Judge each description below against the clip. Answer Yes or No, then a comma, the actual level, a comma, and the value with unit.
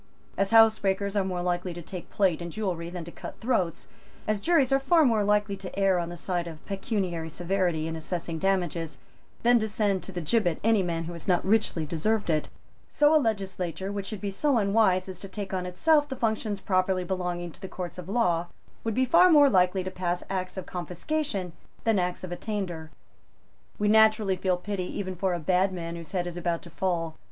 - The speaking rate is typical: No, fast, 210 wpm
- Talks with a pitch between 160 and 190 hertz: Yes, medium, 185 Hz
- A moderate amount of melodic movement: Yes, average, 3.2 semitones